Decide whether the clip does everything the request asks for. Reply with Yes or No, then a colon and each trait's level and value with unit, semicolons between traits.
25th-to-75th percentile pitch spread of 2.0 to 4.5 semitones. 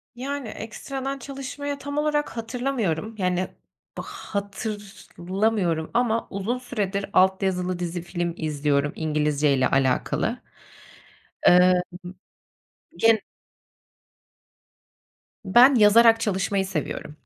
No: wide, 5.5 semitones